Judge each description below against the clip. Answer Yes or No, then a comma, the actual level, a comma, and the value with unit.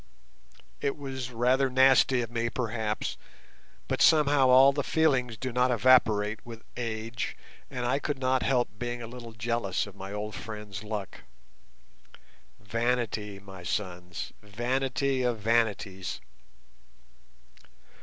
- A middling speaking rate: No, slow, 125 wpm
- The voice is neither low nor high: No, low, 120 Hz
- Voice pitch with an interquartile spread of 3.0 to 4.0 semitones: Yes, average, 3.4 semitones